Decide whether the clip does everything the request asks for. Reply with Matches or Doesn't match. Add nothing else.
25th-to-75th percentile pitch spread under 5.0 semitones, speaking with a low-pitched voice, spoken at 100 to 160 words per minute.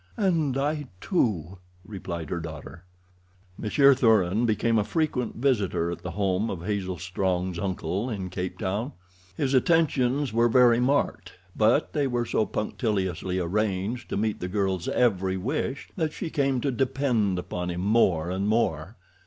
Doesn't match